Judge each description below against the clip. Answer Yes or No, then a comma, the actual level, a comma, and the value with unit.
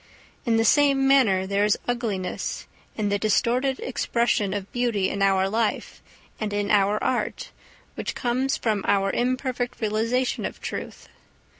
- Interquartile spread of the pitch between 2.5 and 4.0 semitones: Yes, average, 3.5 semitones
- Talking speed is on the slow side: No, average, 145 wpm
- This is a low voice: No, high, 220 Hz